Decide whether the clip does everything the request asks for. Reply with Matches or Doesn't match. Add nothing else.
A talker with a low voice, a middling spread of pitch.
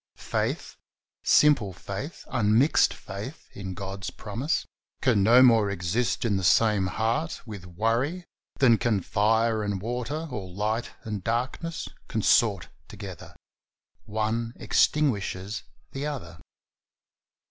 Matches